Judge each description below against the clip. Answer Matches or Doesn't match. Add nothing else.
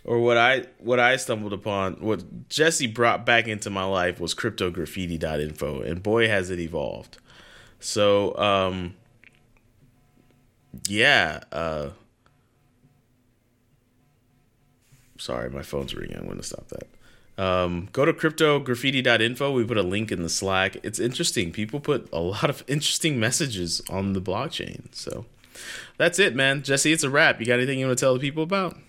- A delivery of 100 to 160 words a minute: Matches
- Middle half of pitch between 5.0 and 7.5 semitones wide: Matches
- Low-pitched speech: Matches